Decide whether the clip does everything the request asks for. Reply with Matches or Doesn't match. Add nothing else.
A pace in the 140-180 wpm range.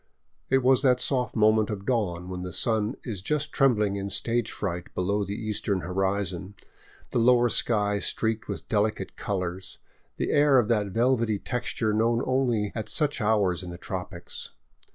Matches